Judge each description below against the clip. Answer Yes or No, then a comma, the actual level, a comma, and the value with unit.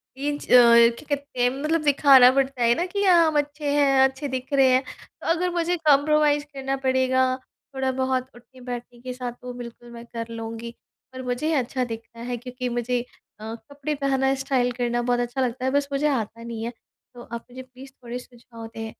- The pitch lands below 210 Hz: No, very high, 255 Hz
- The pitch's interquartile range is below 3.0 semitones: Yes, narrow, 2.5 semitones